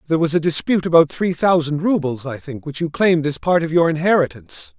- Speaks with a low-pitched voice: No, medium, 155 Hz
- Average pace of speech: No, fast, 225 wpm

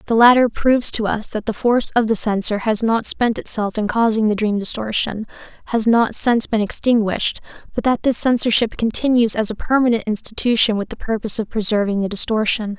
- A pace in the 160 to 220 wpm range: Yes, average, 190 wpm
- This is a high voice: Yes, high, 220 Hz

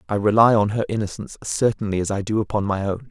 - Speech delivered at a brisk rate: Yes, fast, 250 wpm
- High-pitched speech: No, low, 105 Hz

